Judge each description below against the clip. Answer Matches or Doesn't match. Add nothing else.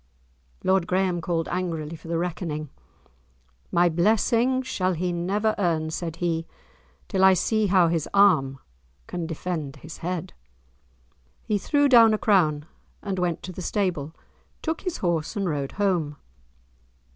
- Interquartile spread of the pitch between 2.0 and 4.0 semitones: Matches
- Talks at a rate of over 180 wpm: Doesn't match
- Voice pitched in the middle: Matches